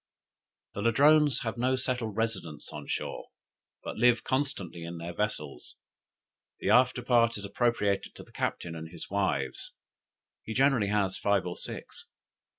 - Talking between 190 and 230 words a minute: No, average, 150 wpm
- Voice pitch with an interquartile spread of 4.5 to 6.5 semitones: Yes, average, 4.8 semitones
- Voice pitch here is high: No, low, 110 Hz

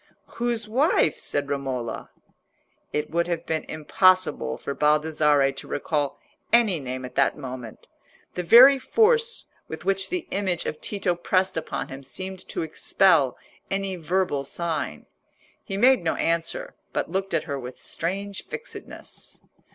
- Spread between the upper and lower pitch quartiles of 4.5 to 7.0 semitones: Yes, wide, 5.4 semitones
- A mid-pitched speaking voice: Yes, medium, 170 Hz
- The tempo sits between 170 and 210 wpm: No, average, 145 wpm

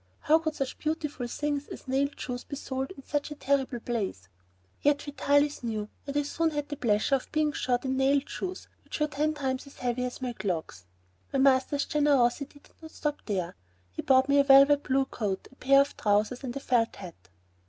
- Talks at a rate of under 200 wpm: No, fast, 205 wpm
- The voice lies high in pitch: Yes, very high, 270 Hz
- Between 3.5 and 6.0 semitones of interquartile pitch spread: No, average, 2.9 semitones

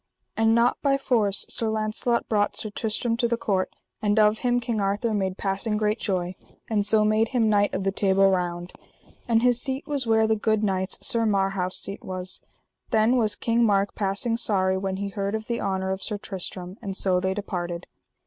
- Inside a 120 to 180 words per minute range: No, average, 200 wpm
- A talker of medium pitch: No, high, 210 Hz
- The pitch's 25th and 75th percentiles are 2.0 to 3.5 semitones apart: Yes, average, 2.7 semitones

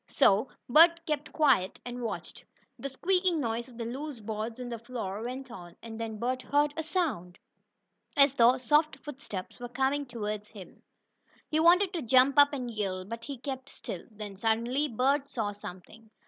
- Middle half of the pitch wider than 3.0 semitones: Yes, average, 4.6 semitones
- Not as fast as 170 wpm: No, average, 175 wpm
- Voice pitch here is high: Yes, high, 245 Hz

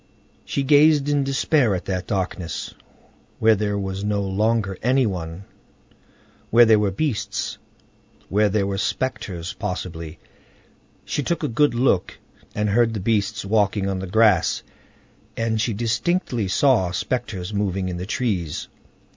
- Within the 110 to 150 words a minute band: Yes, average, 140 wpm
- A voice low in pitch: Yes, low, 105 Hz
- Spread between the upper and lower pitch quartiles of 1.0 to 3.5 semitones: No, average, 3.9 semitones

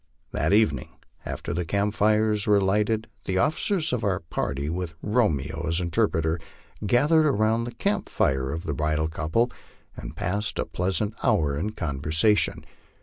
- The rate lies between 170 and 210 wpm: No, average, 150 wpm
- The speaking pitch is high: No, very low, 95 Hz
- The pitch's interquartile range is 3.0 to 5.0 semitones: No, wide, 5.4 semitones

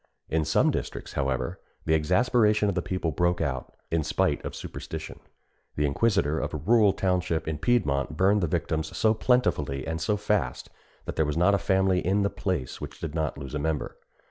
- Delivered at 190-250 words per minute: Yes, average, 195 wpm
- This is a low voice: Yes, very low, 85 Hz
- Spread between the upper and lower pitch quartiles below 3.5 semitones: No, average, 4.7 semitones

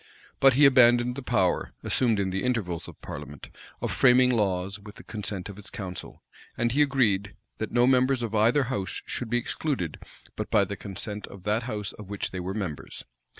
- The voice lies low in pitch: Yes, low, 110 Hz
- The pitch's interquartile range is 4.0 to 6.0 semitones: Yes, average, 4.3 semitones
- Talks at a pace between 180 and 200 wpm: Yes, average, 195 wpm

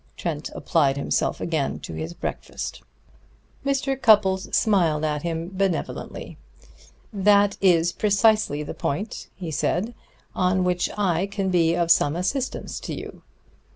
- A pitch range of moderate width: Yes, average, 3.8 semitones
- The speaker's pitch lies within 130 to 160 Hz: No, medium, 180 Hz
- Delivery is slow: Yes, slow, 130 wpm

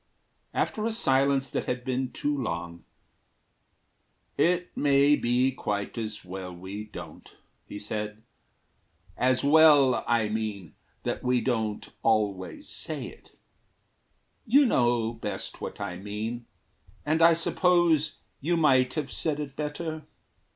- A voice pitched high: No, low, 125 Hz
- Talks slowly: Yes, slow, 125 wpm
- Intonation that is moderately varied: No, wide, 5.7 semitones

